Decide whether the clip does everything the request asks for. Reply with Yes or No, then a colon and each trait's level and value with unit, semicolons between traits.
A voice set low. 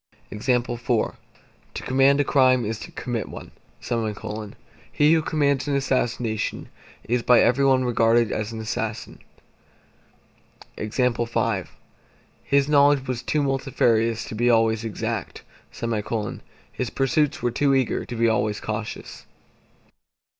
Yes: low, 120 Hz